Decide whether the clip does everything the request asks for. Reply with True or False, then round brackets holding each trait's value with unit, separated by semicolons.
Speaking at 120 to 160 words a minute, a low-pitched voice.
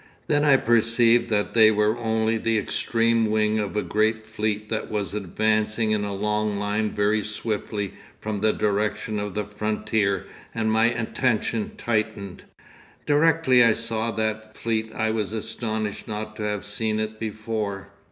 True (155 wpm; 110 Hz)